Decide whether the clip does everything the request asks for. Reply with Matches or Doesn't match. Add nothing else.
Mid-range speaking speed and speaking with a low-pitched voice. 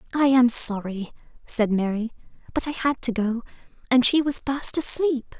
Doesn't match